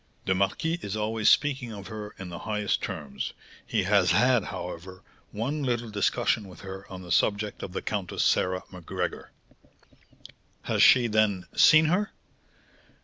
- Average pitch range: Yes, average, 3.7 semitones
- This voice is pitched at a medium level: No, low, 105 Hz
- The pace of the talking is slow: No, average, 150 wpm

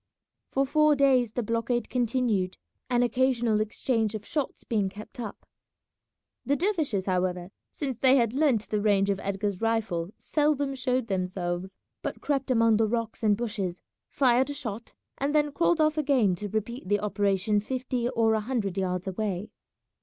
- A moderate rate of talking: Yes, average, 160 wpm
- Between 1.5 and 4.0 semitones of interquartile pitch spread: No, average, 4.5 semitones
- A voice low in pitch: No, high, 225 Hz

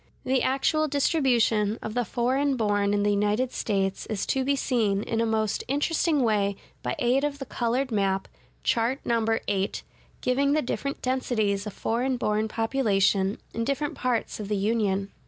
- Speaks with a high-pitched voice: Yes, high, 230 Hz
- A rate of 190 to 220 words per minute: No, average, 175 wpm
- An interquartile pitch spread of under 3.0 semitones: No, average, 4.2 semitones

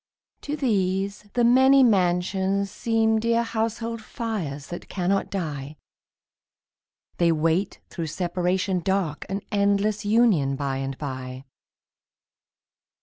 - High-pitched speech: Yes, high, 195 Hz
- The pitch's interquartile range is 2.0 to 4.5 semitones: No, average, 5.2 semitones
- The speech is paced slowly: Yes, slow, 105 wpm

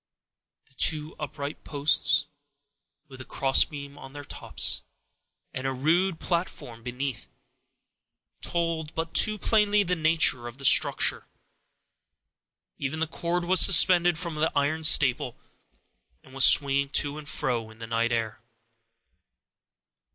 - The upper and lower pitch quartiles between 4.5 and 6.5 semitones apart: No, average, 3.8 semitones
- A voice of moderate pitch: Yes, medium, 145 Hz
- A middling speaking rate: No, slow, 130 wpm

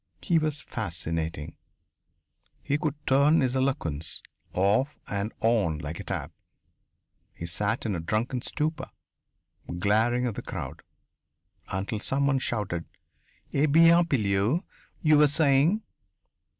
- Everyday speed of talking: No, slow, 120 wpm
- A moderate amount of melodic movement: No, wide, 6.9 semitones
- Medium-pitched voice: No, low, 120 Hz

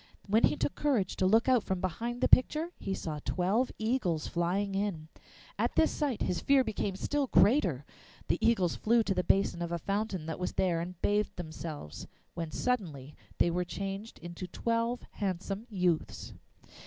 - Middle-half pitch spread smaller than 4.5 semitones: No, average, 4.9 semitones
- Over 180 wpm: No, average, 175 wpm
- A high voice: Yes, high, 195 Hz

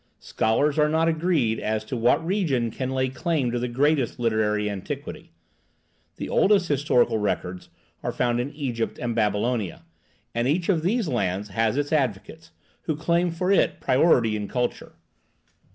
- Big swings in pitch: Yes, wide, 6.0 semitones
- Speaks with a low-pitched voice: Yes, low, 125 Hz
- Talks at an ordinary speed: Yes, average, 155 wpm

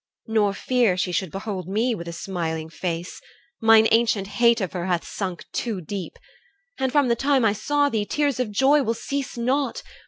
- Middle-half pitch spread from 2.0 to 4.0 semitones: No, average, 5.2 semitones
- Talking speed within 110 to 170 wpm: No, average, 190 wpm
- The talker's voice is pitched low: No, high, 220 Hz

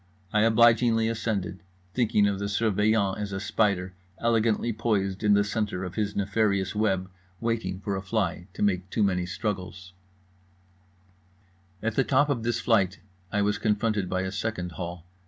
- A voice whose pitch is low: Yes, low, 105 Hz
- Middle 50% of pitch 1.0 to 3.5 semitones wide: Yes, average, 2.8 semitones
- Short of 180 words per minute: Yes, average, 160 wpm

